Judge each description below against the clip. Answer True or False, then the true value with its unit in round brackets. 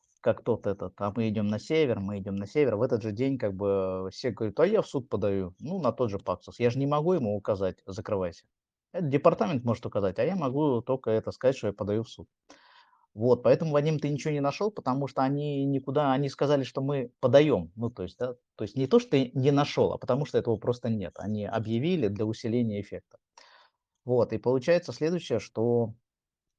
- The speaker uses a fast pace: True (215 wpm)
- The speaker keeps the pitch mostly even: False (5.1 semitones)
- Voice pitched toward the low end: True (125 Hz)